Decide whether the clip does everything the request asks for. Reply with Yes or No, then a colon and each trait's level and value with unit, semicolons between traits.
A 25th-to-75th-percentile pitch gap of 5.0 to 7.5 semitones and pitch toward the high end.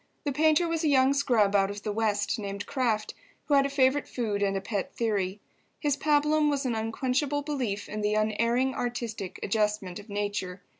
Yes: average, 5.3 semitones; high, 230 Hz